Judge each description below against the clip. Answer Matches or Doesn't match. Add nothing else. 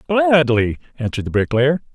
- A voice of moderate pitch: Matches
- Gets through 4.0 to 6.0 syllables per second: Matches